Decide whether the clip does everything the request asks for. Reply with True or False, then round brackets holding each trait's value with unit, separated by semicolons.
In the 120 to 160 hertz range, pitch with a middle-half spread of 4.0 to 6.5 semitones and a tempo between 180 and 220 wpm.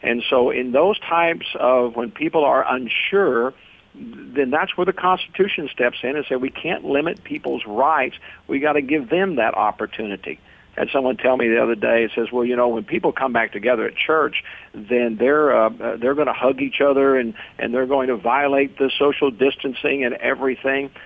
False (135 Hz; 3.6 semitones; 200 wpm)